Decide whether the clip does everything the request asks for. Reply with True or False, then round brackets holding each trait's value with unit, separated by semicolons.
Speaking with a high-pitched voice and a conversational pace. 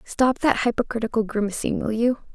True (230 Hz; 155 wpm)